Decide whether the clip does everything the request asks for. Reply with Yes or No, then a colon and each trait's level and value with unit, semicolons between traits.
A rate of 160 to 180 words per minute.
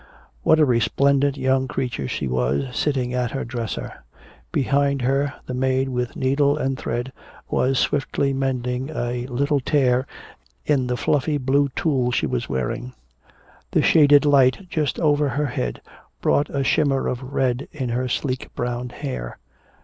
No: average, 150 wpm